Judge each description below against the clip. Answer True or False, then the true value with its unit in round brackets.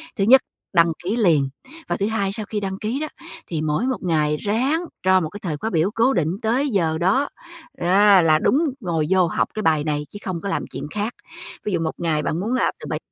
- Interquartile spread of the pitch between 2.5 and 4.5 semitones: False (5.3 semitones)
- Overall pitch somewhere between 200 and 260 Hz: False (190 Hz)